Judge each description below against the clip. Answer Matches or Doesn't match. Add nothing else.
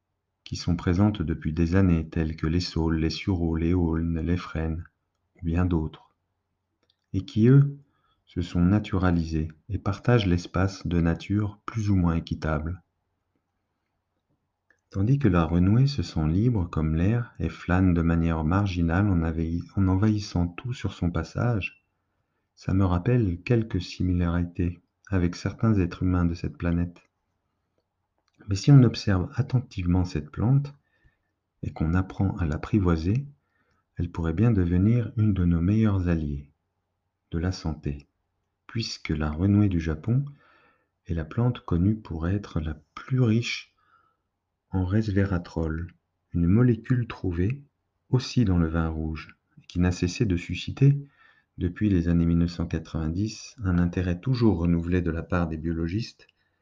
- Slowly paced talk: Matches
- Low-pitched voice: Matches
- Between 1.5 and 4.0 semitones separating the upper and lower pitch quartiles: Matches